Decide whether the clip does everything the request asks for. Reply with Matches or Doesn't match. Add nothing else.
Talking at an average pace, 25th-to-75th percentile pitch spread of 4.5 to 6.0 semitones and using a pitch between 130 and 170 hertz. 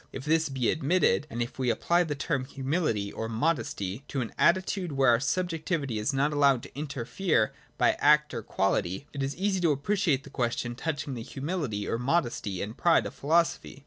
Matches